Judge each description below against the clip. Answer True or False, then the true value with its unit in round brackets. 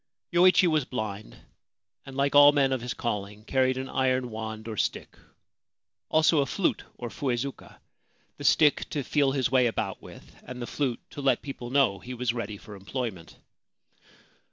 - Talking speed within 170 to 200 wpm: True (180 wpm)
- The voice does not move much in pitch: False (3.3 semitones)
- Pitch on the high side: False (130 Hz)